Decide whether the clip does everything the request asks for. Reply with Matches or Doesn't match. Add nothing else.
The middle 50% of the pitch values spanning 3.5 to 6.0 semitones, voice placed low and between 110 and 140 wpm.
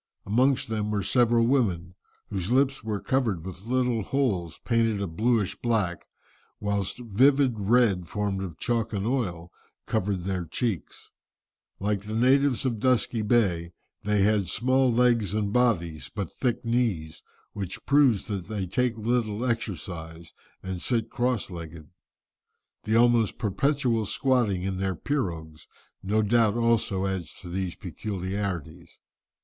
Matches